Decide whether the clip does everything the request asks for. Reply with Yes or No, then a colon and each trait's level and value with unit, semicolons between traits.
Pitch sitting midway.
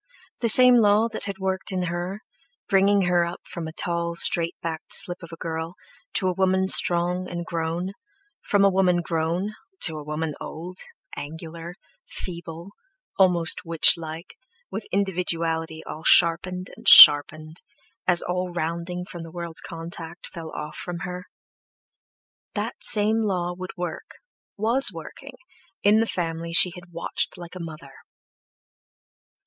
Yes: medium, 175 Hz